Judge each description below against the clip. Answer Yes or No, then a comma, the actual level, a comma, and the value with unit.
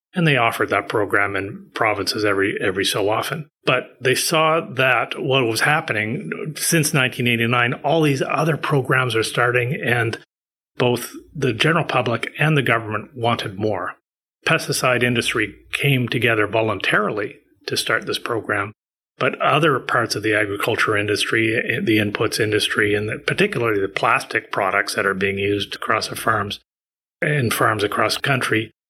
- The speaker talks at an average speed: Yes, average, 150 wpm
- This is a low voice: Yes, low, 120 Hz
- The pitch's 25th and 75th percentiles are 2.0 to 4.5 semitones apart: No, average, 4.9 semitones